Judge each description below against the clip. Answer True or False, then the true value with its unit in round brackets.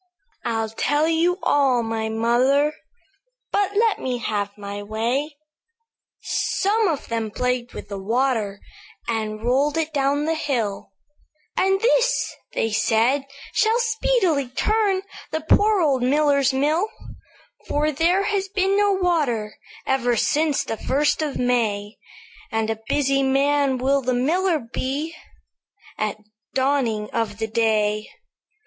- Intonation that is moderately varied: False (6.1 semitones)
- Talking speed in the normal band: False (130 wpm)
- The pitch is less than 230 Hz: False (270 Hz)